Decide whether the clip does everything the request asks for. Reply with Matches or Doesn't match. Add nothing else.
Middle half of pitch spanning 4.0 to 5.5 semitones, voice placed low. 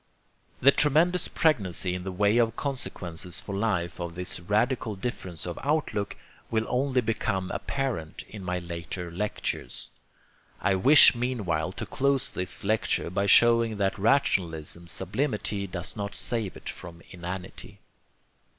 Matches